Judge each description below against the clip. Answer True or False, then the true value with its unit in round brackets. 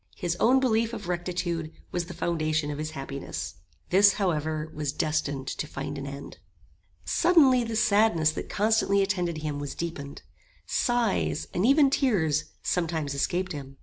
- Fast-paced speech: False (150 wpm)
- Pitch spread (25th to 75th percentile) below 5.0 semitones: False (5.5 semitones)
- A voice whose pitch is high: False (170 Hz)